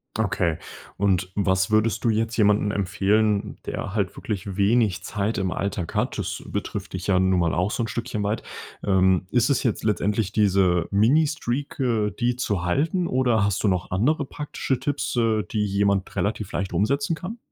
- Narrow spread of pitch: No, average, 3.5 semitones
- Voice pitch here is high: No, low, 105 Hz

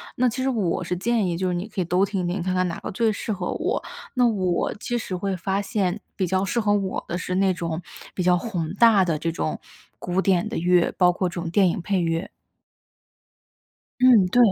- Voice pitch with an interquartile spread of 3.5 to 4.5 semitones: No, average, 2.8 semitones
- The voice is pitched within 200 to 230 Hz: No, medium, 185 Hz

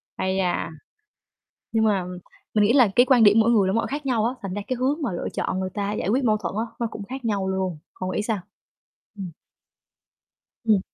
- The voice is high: Yes, high, 215 Hz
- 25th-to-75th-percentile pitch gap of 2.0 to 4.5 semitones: Yes, average, 3.9 semitones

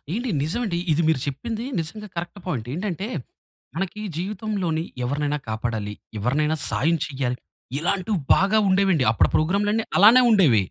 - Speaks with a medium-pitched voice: Yes, medium, 170 Hz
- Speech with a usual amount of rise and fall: No, wide, 6.1 semitones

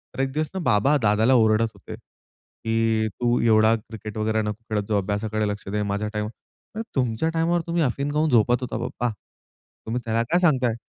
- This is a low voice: Yes, low, 115 Hz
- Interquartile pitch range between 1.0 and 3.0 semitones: No, average, 3.6 semitones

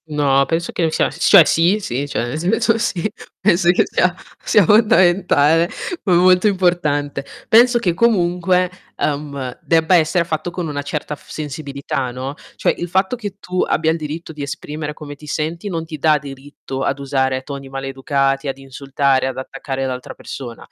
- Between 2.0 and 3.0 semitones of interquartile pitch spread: No, average, 4.4 semitones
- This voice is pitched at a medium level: Yes, medium, 155 Hz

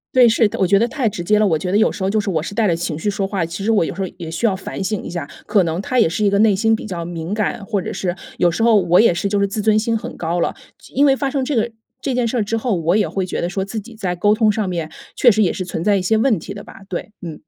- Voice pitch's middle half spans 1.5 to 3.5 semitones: No, average, 3.9 semitones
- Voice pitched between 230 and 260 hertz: No, high, 200 Hz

